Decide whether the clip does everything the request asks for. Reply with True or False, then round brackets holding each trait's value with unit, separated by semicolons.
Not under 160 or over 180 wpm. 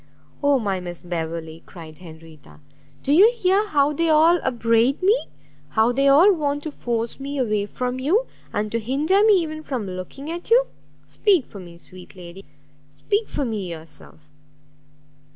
True (165 wpm)